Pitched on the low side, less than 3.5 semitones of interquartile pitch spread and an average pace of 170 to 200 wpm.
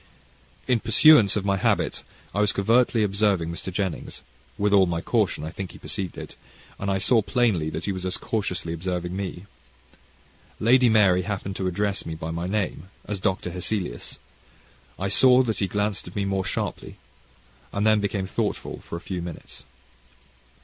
Yes: low, 100 Hz; average, 2.7 semitones; average, 175 wpm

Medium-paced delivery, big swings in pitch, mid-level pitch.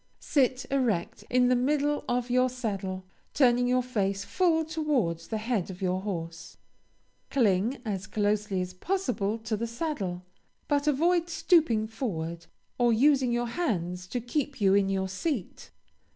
No: average, 150 wpm; wide, 5.9 semitones; high, 235 Hz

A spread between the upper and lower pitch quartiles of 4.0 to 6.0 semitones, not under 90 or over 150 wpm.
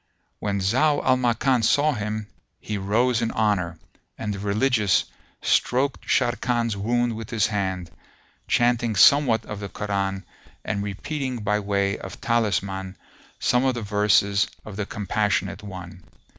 No: average, 3.3 semitones; average, 140 wpm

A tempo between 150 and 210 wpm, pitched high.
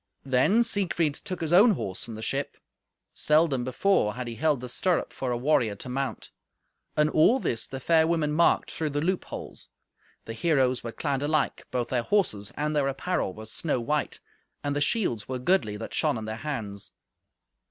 No: average, 185 wpm; medium, 140 Hz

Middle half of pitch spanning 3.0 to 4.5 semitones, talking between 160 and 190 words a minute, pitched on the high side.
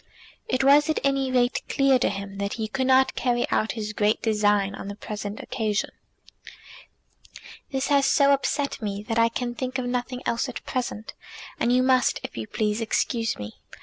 Yes: average, 3.7 semitones; average, 185 wpm; high, 240 Hz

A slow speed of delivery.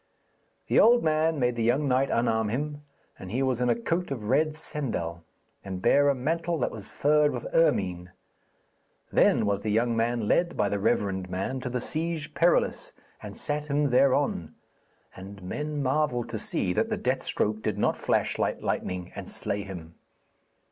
No: average, 180 wpm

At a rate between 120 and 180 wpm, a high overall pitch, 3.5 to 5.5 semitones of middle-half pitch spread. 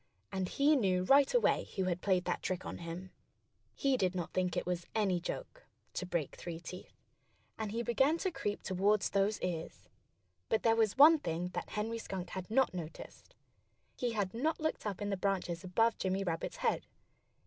No: average, 190 wpm; high, 195 Hz; average, 4.1 semitones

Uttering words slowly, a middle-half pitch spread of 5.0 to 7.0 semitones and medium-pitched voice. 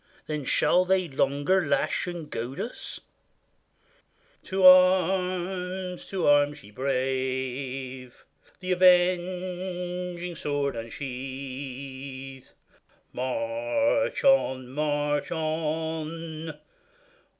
Yes: slow, 75 wpm; average, 5.3 semitones; medium, 155 Hz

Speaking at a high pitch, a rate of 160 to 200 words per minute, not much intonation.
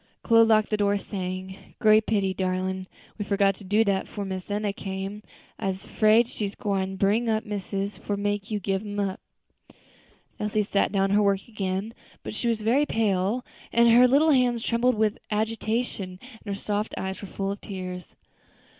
Yes: high, 205 Hz; average, 180 wpm; narrow, 2.2 semitones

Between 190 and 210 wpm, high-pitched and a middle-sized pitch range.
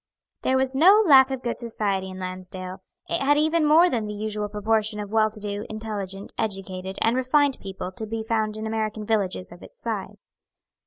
Yes: average, 195 wpm; high, 215 Hz; average, 4.5 semitones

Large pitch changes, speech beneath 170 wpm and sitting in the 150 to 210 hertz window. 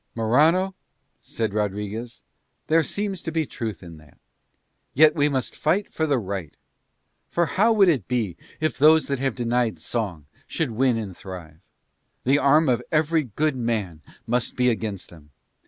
No: wide, 7.0 semitones; average, 160 wpm; low, 125 Hz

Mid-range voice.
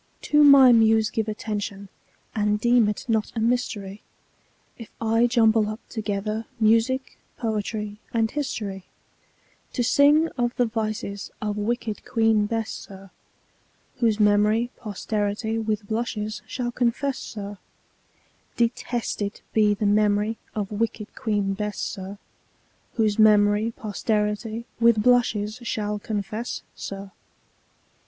No: high, 215 Hz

